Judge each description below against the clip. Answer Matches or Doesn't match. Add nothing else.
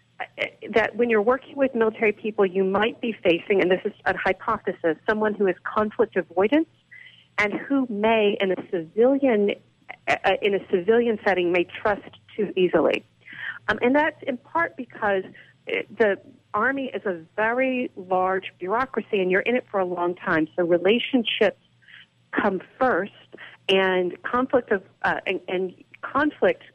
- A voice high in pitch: Matches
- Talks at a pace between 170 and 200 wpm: Doesn't match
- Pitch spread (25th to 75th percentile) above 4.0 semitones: Matches